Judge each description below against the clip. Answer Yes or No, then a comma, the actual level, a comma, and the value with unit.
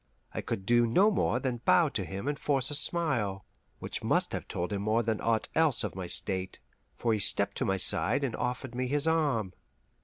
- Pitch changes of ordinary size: No, wide, 6.0 semitones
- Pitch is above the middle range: No, low, 120 Hz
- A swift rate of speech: Yes, fast, 210 wpm